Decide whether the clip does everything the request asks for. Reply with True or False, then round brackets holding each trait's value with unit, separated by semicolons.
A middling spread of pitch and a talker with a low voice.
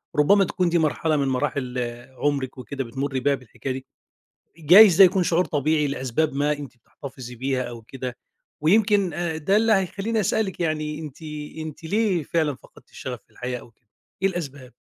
False (4.9 semitones; 150 Hz)